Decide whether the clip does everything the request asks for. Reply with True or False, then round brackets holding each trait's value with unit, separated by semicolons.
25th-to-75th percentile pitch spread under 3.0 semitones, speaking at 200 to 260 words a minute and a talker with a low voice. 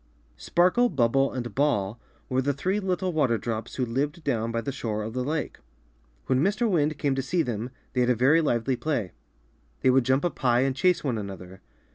False (4.7 semitones; 205 wpm; 130 Hz)